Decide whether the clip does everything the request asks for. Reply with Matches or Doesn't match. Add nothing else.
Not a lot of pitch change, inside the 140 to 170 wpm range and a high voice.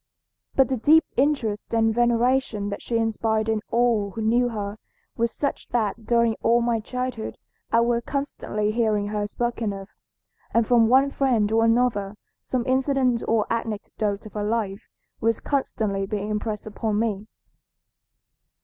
Matches